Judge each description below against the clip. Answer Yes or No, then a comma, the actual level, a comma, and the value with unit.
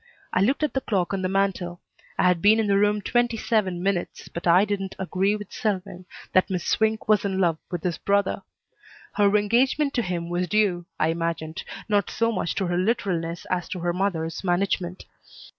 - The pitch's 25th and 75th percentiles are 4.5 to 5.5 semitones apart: No, average, 2.9 semitones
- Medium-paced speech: Yes, average, 195 wpm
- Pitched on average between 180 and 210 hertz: Yes, high, 190 Hz